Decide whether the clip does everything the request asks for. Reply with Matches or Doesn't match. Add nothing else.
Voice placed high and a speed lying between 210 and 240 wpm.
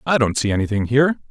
Doesn't match